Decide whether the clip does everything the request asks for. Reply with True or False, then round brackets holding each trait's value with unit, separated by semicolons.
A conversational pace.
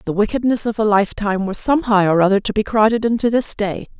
False (225 wpm)